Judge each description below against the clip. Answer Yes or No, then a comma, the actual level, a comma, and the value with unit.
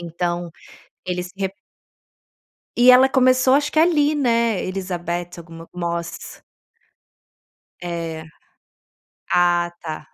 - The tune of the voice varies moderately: No, wide, 6.7 semitones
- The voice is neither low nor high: Yes, medium, 180 Hz